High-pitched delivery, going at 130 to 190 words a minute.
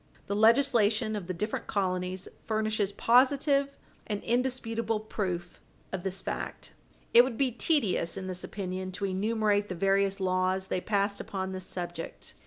Yes: high, 200 Hz; average, 150 wpm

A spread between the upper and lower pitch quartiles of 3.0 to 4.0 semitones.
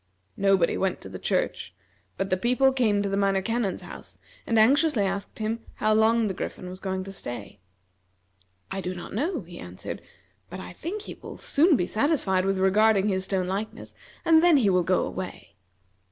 Yes: average, 3.6 semitones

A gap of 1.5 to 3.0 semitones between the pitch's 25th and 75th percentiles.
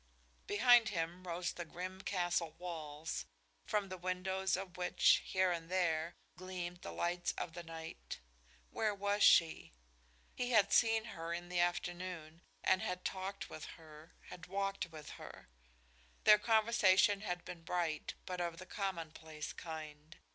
Yes: narrow, 2.6 semitones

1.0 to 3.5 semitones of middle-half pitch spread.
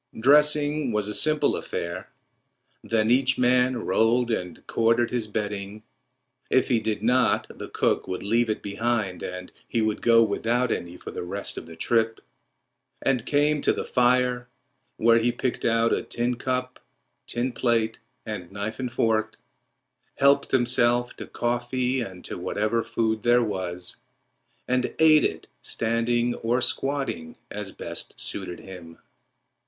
Yes: average, 2.9 semitones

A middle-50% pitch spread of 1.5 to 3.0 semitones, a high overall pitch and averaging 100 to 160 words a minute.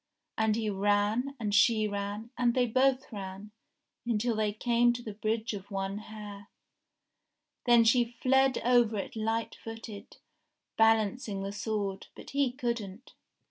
Yes: average, 2.7 semitones; high, 220 Hz; average, 140 wpm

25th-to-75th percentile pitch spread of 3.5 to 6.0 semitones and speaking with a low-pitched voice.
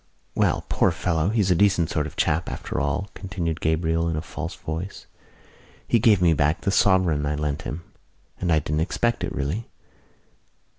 Yes: average, 3.8 semitones; very low, 85 Hz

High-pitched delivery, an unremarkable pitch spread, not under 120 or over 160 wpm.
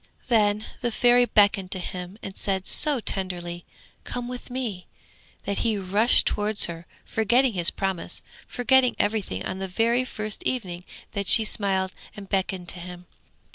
Yes: high, 205 Hz; average, 4.1 semitones; average, 155 wpm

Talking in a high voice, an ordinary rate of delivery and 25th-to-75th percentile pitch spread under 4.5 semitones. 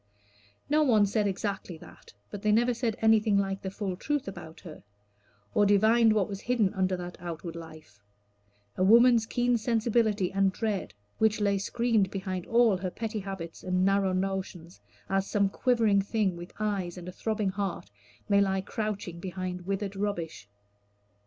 Yes: high, 200 Hz; average, 160 wpm; average, 2.8 semitones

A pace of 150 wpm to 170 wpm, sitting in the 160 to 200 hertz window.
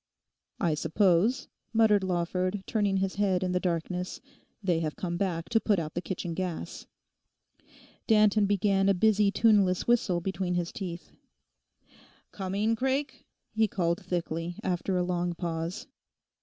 No: average, 140 wpm; medium, 185 Hz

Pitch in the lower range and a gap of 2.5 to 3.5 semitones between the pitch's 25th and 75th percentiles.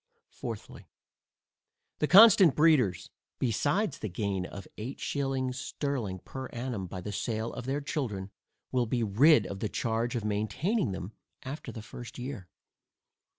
No: low, 120 Hz; average, 5.3 semitones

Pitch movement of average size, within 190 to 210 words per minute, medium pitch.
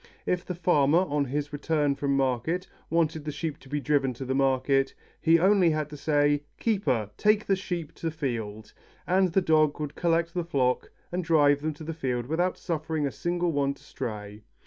Yes: average, 3.5 semitones; average, 195 wpm; medium, 150 Hz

